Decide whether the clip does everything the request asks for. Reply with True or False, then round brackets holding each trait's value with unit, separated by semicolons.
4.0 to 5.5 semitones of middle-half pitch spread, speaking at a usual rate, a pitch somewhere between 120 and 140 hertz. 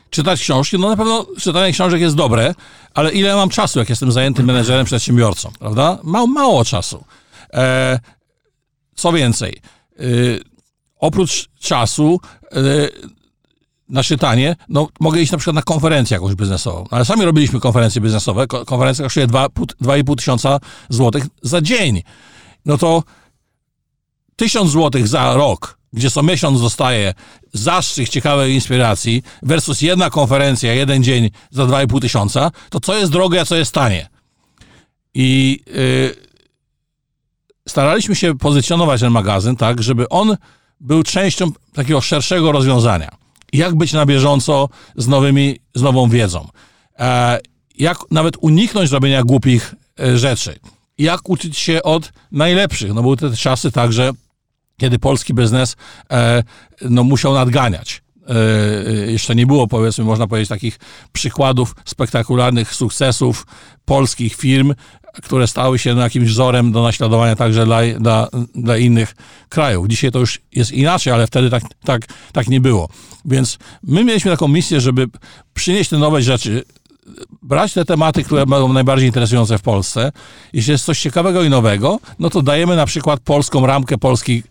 True (4.4 semitones; 140 wpm; 130 Hz)